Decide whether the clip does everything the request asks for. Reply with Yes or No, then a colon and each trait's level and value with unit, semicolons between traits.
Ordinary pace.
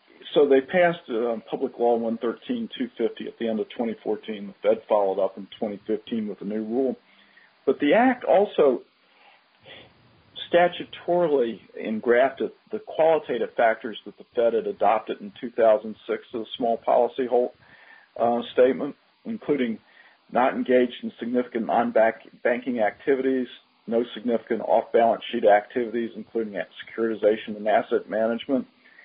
No: slow, 130 wpm